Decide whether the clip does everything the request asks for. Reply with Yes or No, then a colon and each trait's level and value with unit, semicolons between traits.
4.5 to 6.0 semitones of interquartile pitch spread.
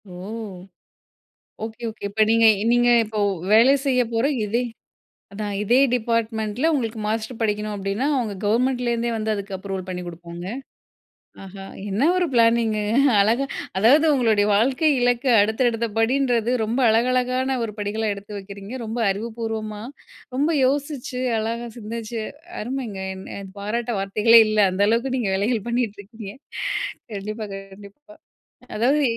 No: average, 2.8 semitones